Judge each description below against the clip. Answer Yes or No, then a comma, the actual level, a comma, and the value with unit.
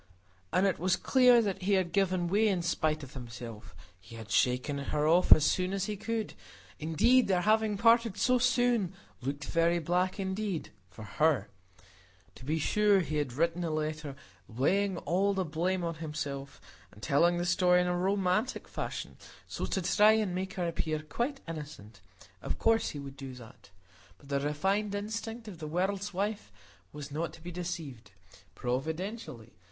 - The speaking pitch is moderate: Yes, medium, 175 Hz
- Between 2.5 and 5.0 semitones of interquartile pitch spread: No, wide, 5.4 semitones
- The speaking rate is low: No, average, 175 wpm